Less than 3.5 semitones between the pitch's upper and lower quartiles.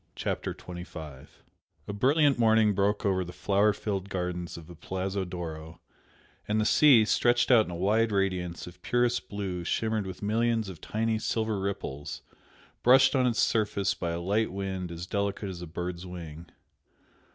No: average, 3.8 semitones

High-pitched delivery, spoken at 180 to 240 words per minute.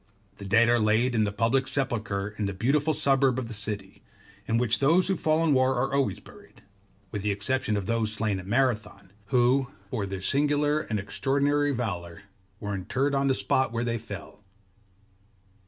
No: low, 115 Hz; average, 185 wpm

